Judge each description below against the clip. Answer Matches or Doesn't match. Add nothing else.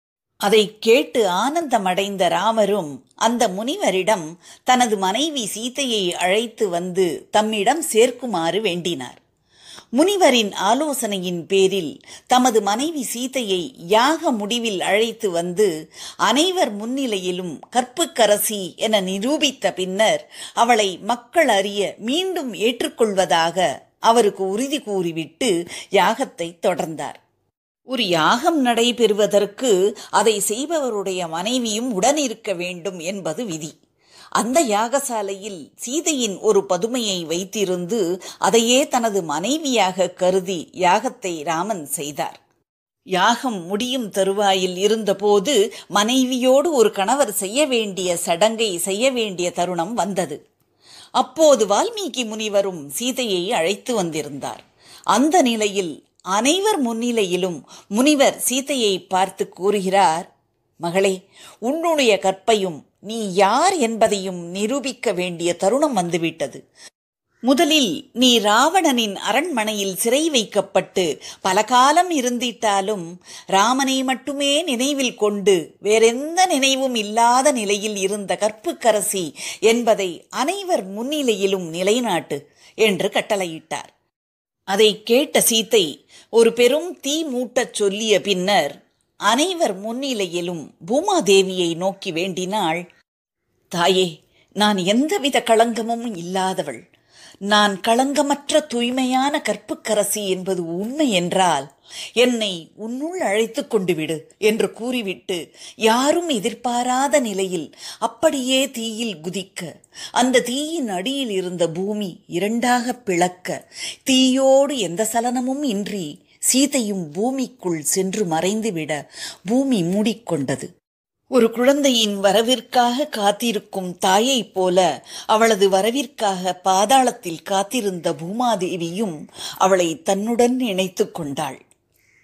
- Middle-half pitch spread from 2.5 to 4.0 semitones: Doesn't match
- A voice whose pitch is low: Doesn't match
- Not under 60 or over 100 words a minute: Matches